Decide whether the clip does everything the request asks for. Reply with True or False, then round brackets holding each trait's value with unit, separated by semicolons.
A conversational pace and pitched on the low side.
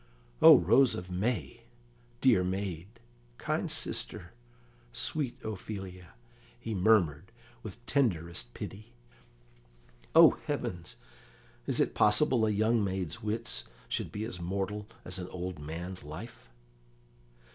False (115 wpm; 95 Hz)